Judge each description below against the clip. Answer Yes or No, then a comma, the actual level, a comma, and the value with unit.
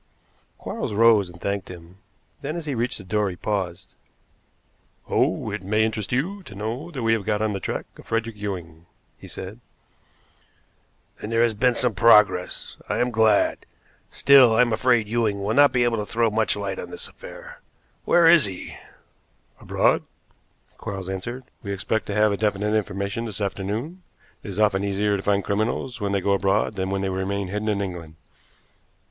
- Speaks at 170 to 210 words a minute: Yes, average, 185 wpm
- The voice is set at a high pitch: No, low, 105 Hz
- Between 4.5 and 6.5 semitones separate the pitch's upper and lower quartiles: No, average, 2.8 semitones